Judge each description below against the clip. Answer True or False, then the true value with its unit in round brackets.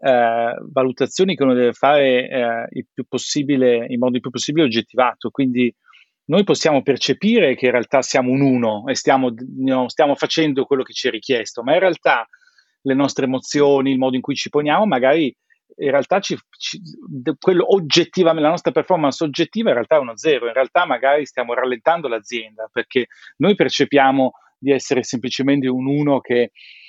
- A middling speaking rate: False (175 wpm)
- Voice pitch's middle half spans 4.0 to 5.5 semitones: False (3.2 semitones)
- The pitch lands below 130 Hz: False (135 Hz)